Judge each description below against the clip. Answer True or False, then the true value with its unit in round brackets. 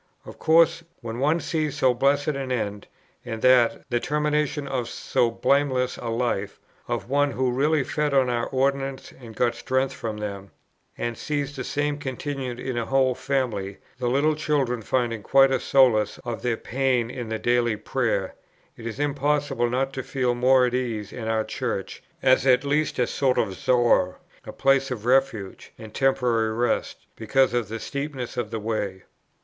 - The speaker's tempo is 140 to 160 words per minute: False (175 wpm)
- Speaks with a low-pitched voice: True (125 Hz)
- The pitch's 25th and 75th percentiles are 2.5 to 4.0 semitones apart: True (2.9 semitones)